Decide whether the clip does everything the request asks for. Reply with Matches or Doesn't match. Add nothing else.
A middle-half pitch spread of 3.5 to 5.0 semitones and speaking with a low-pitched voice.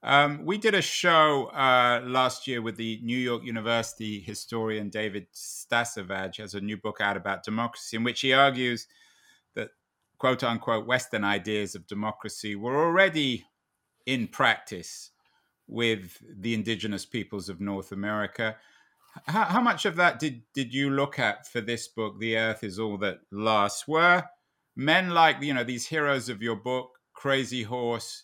Matches